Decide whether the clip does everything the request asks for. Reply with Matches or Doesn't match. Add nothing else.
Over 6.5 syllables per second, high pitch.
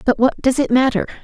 Doesn't match